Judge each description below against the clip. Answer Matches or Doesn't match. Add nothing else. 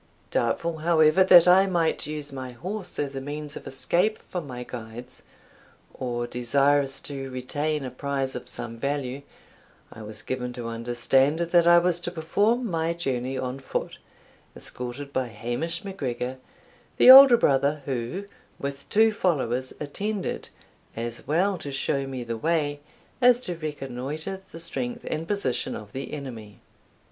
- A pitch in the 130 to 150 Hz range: Matches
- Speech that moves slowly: Doesn't match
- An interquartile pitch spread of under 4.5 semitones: Doesn't match